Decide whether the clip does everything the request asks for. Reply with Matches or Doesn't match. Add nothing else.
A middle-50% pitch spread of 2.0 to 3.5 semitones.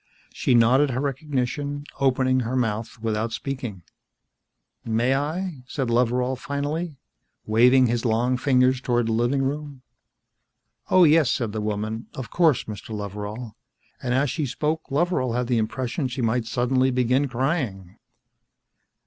Matches